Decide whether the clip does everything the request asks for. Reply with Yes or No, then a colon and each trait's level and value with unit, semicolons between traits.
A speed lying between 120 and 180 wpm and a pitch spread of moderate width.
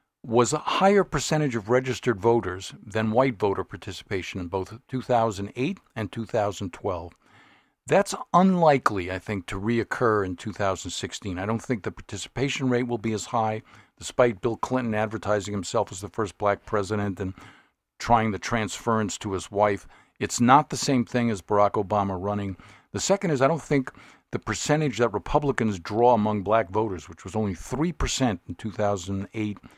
Yes: average, 160 wpm; average, 3.8 semitones